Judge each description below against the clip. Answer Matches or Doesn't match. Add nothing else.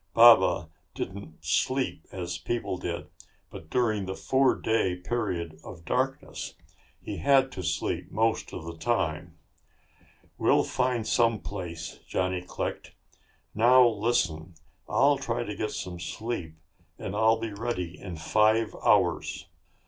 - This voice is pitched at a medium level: Doesn't match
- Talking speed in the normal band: Doesn't match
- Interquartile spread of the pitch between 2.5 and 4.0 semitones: Doesn't match